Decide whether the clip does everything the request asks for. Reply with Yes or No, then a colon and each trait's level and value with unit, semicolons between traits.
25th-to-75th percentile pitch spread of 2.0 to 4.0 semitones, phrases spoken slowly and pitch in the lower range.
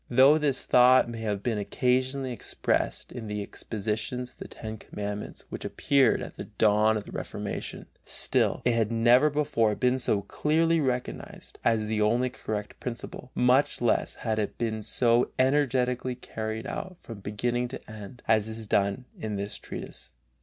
No: average, 2.9 semitones; average, 165 wpm; low, 120 Hz